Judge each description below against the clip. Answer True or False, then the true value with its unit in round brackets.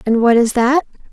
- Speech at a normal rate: False (215 wpm)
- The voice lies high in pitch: True (245 Hz)